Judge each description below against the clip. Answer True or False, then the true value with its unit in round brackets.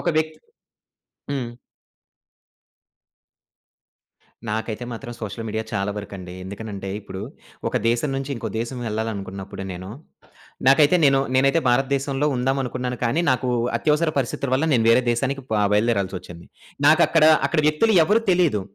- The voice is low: True (120 Hz)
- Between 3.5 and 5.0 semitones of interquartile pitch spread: True (4.7 semitones)